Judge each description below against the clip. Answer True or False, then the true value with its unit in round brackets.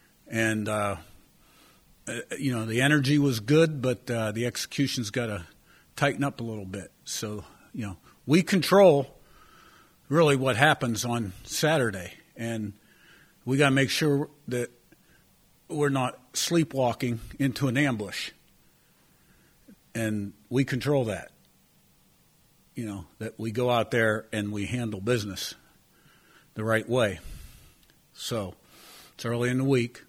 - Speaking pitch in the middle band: False (120 Hz)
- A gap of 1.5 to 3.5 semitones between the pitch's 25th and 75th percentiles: False (4.3 semitones)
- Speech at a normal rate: False (130 wpm)